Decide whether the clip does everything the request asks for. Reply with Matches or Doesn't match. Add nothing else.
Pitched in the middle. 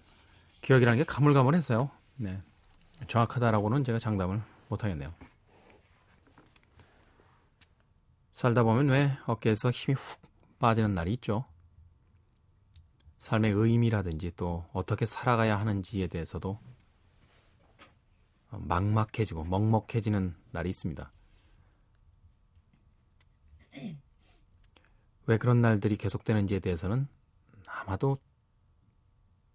Doesn't match